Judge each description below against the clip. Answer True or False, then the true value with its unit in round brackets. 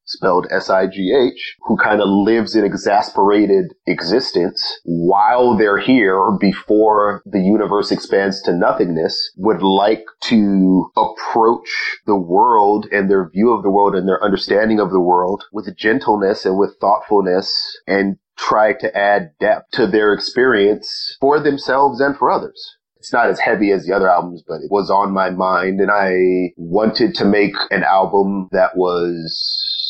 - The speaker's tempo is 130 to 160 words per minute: True (155 wpm)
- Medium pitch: False (100 Hz)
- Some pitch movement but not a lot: False (2.3 semitones)